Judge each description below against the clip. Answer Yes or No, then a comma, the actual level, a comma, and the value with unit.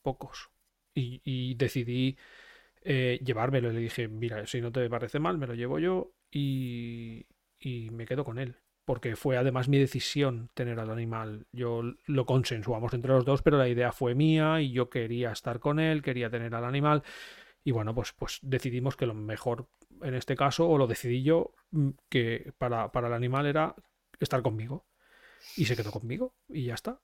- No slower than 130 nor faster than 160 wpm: No, average, 185 wpm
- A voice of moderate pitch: No, low, 130 Hz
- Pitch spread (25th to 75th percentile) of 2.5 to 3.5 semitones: Yes, average, 2.8 semitones